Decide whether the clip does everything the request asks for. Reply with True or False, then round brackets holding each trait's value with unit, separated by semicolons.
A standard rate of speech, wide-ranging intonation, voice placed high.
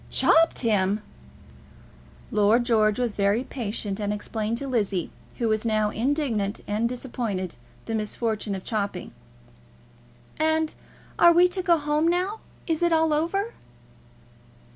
False (130 wpm; 7.0 semitones; 230 Hz)